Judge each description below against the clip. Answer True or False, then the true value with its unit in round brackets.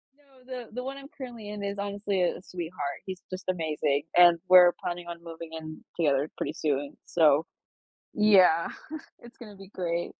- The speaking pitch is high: False (180 Hz)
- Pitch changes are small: False (4.2 semitones)